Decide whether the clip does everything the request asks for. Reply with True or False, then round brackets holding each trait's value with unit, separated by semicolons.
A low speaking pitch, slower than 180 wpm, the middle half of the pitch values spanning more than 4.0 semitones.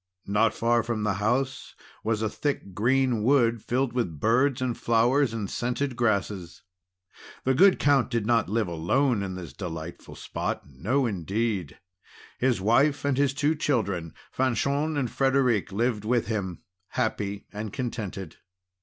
True (115 Hz; 145 wpm; 4.6 semitones)